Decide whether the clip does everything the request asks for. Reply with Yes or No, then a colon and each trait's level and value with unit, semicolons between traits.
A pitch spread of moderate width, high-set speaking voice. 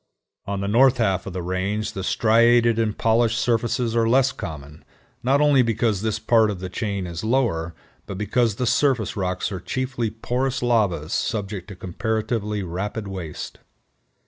No: average, 3.8 semitones; low, 110 Hz